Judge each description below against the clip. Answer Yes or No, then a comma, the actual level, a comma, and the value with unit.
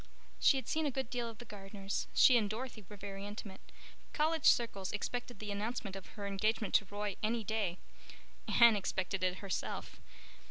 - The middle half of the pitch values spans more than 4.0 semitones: No, average, 3.1 semitones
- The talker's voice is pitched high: Yes, high, 210 Hz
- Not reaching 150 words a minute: No, average, 175 wpm